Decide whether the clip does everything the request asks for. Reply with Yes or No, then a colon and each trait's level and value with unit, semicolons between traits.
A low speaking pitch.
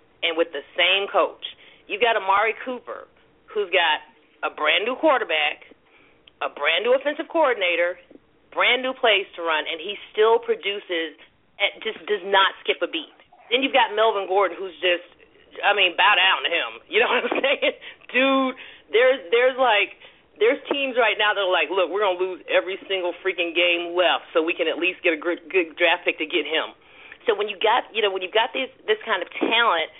No: high, 215 Hz